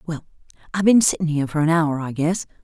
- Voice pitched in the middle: Yes, medium, 160 Hz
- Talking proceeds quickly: Yes, fast, 225 wpm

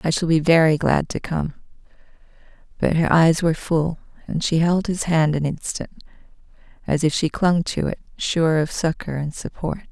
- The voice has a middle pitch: Yes, medium, 160 Hz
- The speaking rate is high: No, average, 180 wpm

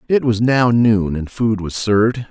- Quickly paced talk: Yes, fast, 210 wpm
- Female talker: No, male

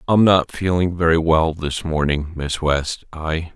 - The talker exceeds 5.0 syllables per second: No, 3.9 syllables/s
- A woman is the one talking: No, male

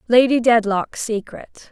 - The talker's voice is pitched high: Yes, high, 230 Hz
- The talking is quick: No, slow, 105 wpm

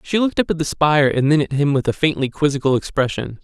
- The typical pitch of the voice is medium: Yes, medium, 150 Hz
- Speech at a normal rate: No, fast, 260 wpm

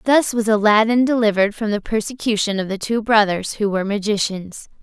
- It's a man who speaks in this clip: No, female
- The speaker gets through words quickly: No, average, 175 wpm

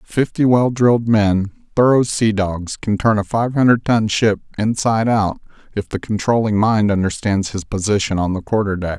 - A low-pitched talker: Yes, low, 105 Hz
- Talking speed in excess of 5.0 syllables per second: No, 4.9 syllables/s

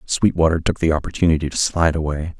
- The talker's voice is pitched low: Yes, very low, 80 Hz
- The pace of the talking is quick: No, average, 175 wpm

